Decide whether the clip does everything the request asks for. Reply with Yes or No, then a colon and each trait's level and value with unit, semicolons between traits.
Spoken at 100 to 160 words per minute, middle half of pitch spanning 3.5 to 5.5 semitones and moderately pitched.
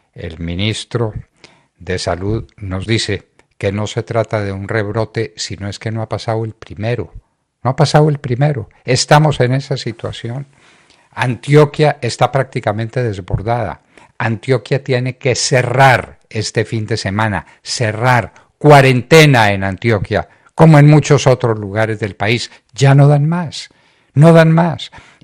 No: average, 145 wpm; average, 4.1 semitones; low, 115 Hz